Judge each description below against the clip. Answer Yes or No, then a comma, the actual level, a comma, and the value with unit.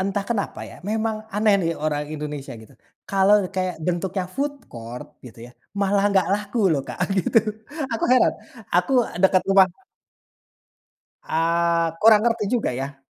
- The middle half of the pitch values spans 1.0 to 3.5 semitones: No, average, 4.3 semitones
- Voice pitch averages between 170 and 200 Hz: Yes, high, 190 Hz